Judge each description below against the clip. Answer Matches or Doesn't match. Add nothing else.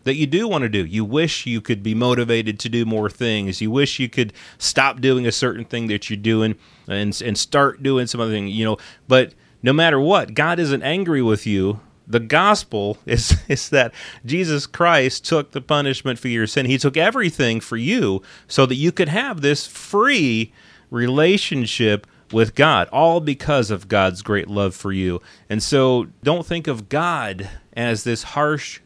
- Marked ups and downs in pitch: Doesn't match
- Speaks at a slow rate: Doesn't match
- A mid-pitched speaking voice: Doesn't match